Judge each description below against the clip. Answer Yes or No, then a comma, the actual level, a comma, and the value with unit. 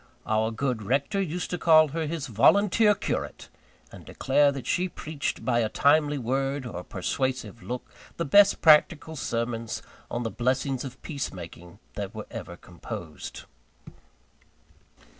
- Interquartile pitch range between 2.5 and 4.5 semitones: No, average, 5.3 semitones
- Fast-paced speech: No, average, 145 wpm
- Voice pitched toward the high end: No, low, 135 Hz